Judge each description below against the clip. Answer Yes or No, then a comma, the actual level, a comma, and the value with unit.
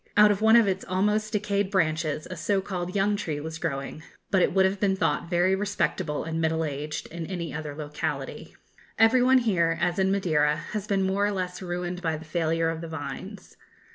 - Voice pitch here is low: No, medium, 180 Hz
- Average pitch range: Yes, average, 3.8 semitones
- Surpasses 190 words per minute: Yes, fast, 205 wpm